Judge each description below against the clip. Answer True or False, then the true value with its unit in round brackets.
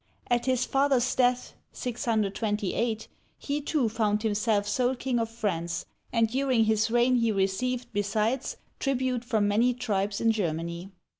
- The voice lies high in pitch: True (230 Hz)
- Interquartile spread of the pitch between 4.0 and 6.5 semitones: False (3.2 semitones)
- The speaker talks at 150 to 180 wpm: False (140 wpm)